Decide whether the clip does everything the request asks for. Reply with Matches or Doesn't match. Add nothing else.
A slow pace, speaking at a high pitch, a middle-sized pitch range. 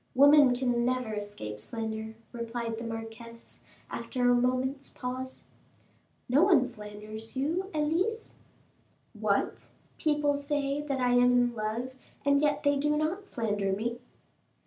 Matches